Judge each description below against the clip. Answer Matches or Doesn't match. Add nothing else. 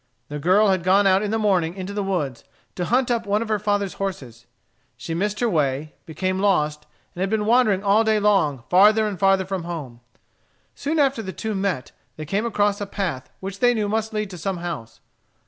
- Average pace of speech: Doesn't match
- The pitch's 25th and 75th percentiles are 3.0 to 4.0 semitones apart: Matches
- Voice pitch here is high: Matches